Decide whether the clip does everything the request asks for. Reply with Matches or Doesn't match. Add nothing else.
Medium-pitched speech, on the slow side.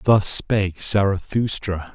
Doesn't match